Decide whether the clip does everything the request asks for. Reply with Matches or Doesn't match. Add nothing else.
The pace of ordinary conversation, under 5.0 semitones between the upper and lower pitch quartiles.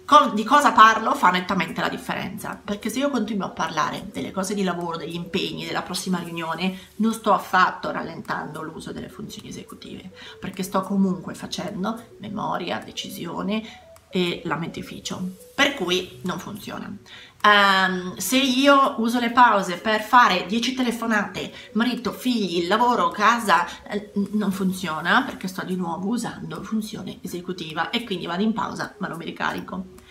Matches